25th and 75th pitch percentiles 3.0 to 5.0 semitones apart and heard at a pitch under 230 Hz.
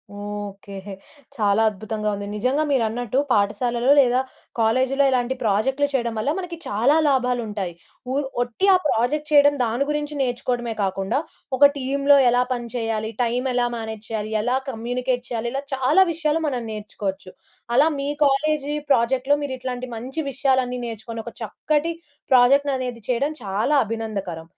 No: average, 3.6 semitones; high, 245 Hz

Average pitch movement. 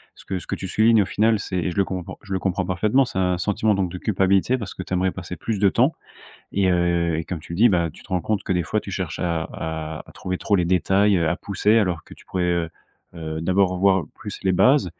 No: narrow, 2.3 semitones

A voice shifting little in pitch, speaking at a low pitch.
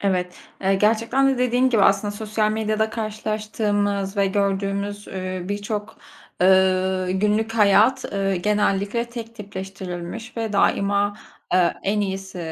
No: narrow, 2.0 semitones; high, 205 Hz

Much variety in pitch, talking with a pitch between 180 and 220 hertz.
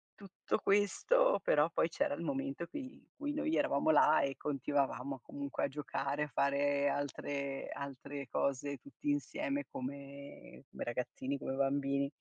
No: wide, 6.9 semitones; medium, 145 Hz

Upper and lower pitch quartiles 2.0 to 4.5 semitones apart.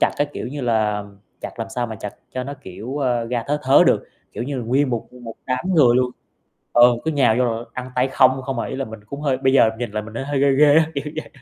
Yes: average, 3.0 semitones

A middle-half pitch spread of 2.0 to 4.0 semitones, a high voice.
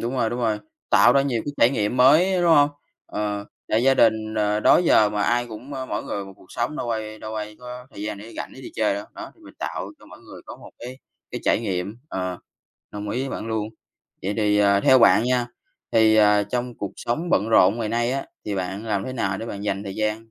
No: average, 3.2 semitones; low, 110 Hz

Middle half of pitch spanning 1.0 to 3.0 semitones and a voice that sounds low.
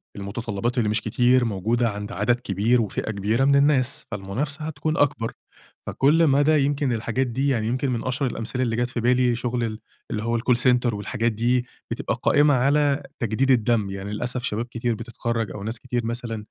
Yes: average, 2.7 semitones; low, 120 Hz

